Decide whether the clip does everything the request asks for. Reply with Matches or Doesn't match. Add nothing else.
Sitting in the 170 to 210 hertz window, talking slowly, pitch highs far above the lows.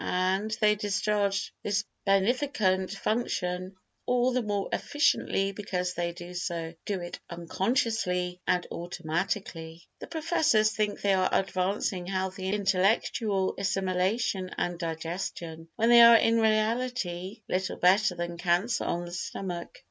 Doesn't match